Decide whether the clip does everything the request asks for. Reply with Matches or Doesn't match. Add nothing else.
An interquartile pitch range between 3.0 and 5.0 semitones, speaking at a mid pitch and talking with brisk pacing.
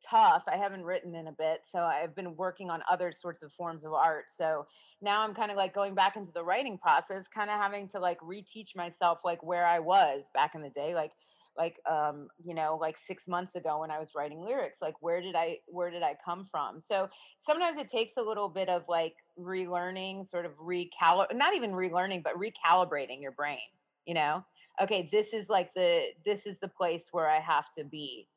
Matches